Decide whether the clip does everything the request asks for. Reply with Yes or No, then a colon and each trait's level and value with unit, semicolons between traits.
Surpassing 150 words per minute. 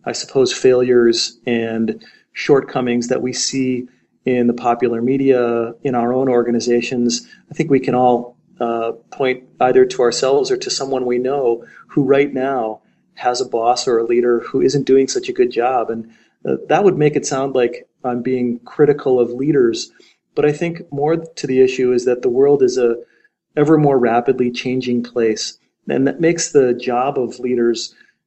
Yes: average, 180 wpm